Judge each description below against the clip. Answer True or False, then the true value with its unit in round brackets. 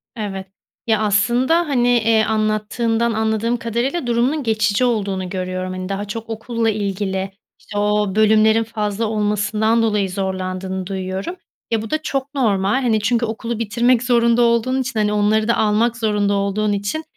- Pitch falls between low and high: False (215 Hz)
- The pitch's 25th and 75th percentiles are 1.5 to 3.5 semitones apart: True (2.5 semitones)